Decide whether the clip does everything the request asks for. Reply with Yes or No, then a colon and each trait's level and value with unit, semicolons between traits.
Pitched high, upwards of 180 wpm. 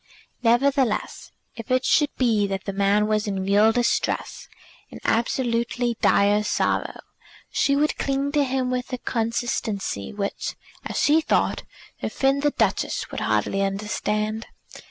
No: high, 230 Hz; average, 140 wpm